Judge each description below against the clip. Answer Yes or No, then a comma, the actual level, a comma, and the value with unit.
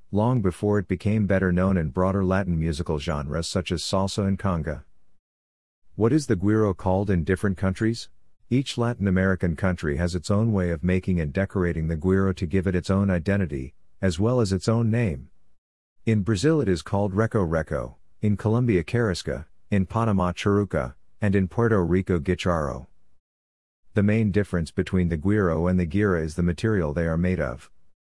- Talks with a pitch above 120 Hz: No, very low, 95 Hz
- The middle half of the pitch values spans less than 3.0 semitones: No, average, 3.4 semitones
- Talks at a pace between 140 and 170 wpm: No, average, 180 wpm